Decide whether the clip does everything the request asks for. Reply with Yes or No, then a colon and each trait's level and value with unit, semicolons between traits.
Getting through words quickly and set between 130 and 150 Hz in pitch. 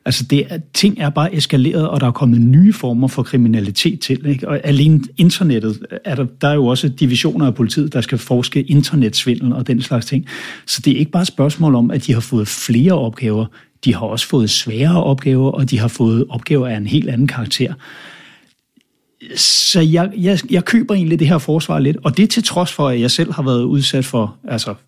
Yes: fast, 215 wpm; low, 135 Hz